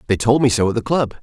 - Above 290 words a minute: Yes, fast, 345 wpm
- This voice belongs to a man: Yes, male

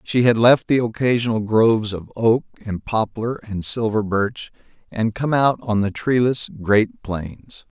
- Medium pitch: No, low, 110 Hz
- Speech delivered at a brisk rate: No, average, 160 wpm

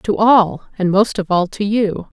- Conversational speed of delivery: No, fast, 220 wpm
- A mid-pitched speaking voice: No, high, 195 Hz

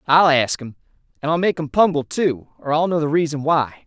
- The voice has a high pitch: No, medium, 150 Hz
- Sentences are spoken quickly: Yes, fast, 235 wpm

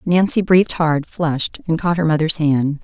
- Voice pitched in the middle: Yes, medium, 160 Hz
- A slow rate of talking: No, average, 190 wpm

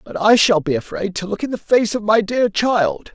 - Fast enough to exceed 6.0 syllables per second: No, 4.9 syllables/s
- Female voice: No, male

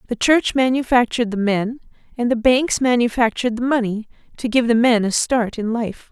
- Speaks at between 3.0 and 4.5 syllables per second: No, 5.3 syllables/s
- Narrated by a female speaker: Yes, female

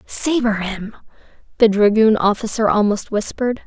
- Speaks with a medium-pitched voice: No, high, 215 Hz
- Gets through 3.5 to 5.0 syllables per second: Yes, 4.8 syllables/s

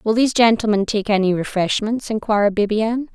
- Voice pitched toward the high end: Yes, high, 215 Hz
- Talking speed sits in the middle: Yes, average, 155 wpm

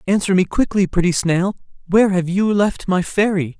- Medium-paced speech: Yes, average, 185 wpm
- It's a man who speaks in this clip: Yes, male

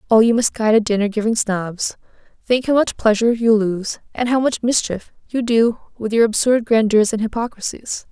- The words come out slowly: No, average, 175 wpm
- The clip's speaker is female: Yes, female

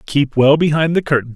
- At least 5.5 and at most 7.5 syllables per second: Yes, 5.7 syllables/s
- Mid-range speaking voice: Yes, medium, 145 Hz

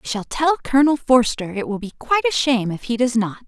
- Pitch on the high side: Yes, high, 245 Hz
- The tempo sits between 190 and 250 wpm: No, fast, 260 wpm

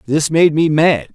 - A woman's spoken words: No, male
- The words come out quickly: Yes, fast, 210 wpm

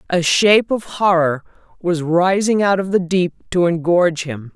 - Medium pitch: Yes, medium, 180 Hz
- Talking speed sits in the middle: Yes, average, 170 wpm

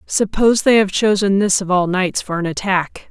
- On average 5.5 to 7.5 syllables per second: No, 5.0 syllables/s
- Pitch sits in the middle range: No, high, 195 Hz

